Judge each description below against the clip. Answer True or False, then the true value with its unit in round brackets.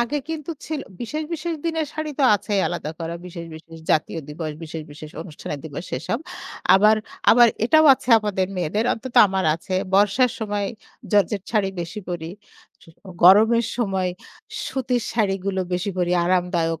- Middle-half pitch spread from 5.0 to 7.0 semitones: True (5.6 semitones)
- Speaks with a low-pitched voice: False (195 Hz)